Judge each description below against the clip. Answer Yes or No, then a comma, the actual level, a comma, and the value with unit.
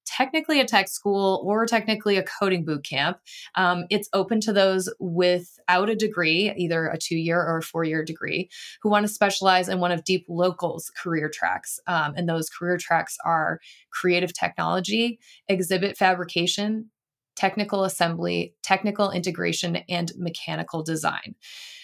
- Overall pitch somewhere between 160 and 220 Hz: Yes, medium, 185 Hz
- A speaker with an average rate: Yes, average, 150 wpm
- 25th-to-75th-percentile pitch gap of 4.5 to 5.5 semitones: No, average, 2.9 semitones